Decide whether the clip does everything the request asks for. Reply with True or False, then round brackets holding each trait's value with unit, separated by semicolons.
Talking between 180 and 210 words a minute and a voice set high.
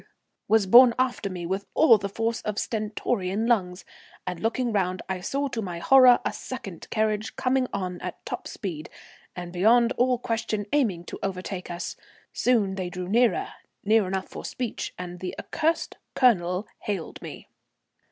False (160 wpm; 205 Hz)